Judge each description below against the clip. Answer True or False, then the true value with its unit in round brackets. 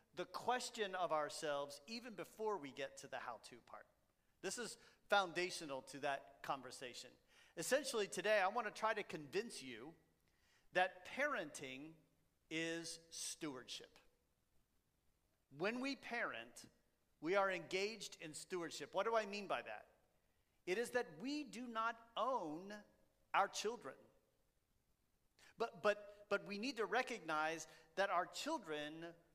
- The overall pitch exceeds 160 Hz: True (185 Hz)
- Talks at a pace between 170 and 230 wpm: False (135 wpm)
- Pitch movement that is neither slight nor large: False (6.1 semitones)